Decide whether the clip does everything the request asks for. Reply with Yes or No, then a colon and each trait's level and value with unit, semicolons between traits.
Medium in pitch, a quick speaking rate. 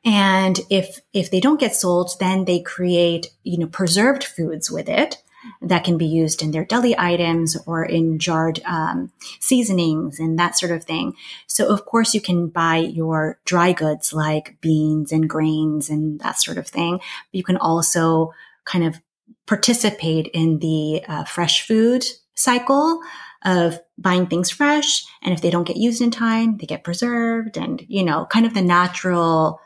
No: medium, 175 Hz; average, 175 wpm